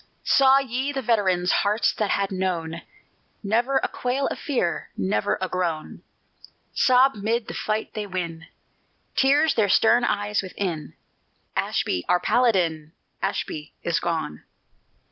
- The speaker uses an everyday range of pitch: No, wide, 6.1 semitones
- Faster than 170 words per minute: No, slow, 135 wpm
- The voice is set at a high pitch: Yes, high, 200 Hz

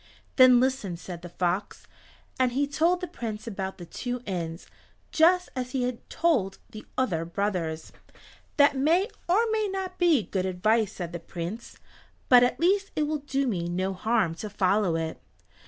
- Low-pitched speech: No, high, 230 Hz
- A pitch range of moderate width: No, wide, 7.8 semitones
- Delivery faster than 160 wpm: Yes, average, 170 wpm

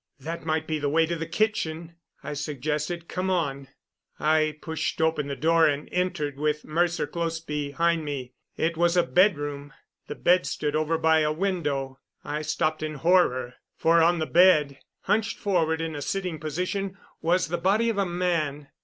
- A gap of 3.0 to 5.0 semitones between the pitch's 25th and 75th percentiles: No, narrow, 2.6 semitones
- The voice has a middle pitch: Yes, medium, 160 Hz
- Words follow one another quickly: No, average, 175 wpm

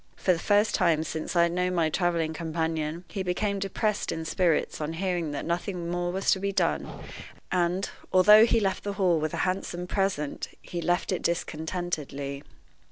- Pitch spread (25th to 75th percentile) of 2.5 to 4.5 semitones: Yes, average, 2.8 semitones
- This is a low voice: No, medium, 175 Hz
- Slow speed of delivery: No, average, 180 wpm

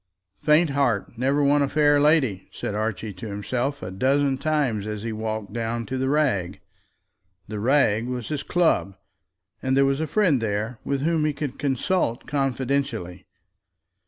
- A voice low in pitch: Yes, low, 130 Hz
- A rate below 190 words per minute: Yes, average, 160 wpm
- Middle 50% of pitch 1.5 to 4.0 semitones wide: No, average, 4.9 semitones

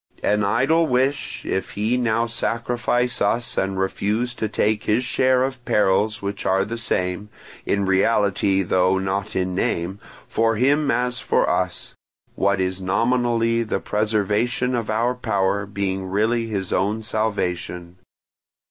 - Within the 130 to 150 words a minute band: Yes, average, 140 wpm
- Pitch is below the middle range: Yes, low, 105 Hz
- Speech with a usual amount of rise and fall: Yes, average, 3.7 semitones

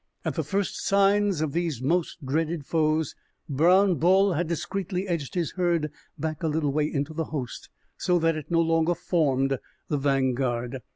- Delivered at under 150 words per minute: No, average, 170 wpm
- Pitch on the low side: No, medium, 160 Hz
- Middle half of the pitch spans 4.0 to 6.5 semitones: No, average, 3.6 semitones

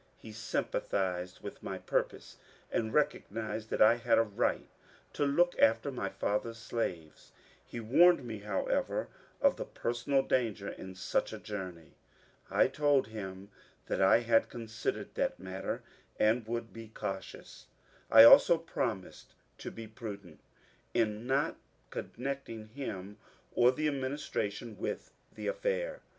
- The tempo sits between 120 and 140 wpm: Yes, slow, 135 wpm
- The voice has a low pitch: Yes, low, 115 Hz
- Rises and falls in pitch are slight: No, average, 4.2 semitones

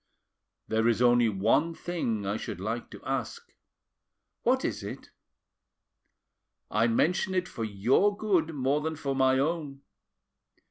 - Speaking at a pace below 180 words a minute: Yes, slow, 135 wpm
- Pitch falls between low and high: No, low, 130 Hz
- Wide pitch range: Yes, wide, 6.2 semitones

